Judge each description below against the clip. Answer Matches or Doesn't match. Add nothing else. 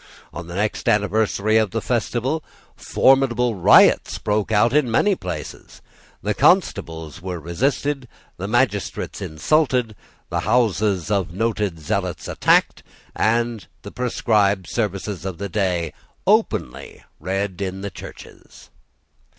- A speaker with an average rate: Doesn't match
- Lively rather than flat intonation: Doesn't match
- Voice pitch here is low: Matches